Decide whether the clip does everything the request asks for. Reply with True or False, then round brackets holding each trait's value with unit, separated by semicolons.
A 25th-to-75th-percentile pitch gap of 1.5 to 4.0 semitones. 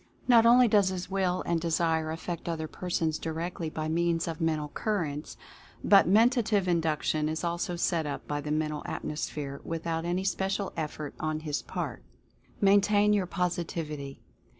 True (3.3 semitones)